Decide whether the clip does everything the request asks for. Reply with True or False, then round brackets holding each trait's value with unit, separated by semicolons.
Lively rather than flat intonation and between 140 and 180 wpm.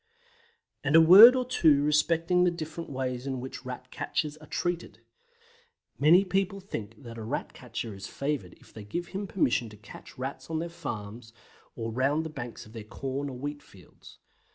False (5.7 semitones; 190 wpm)